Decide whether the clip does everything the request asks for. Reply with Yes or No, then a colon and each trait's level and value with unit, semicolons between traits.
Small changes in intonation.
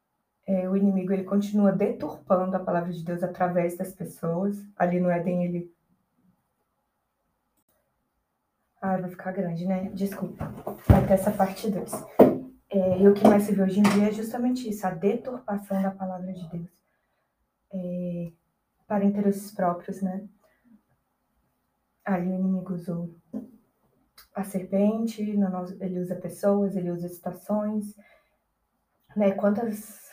Yes: narrow, 2.1 semitones